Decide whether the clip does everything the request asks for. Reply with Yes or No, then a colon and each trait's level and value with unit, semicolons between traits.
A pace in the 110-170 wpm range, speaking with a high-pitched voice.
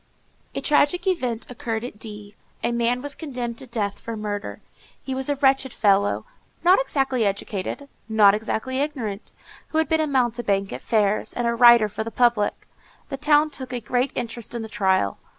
No: average, 185 wpm; high, 235 Hz